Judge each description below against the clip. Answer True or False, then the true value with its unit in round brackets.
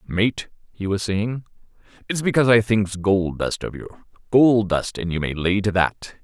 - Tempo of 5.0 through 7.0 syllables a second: False (4.4 syllables/s)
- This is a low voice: True (105 Hz)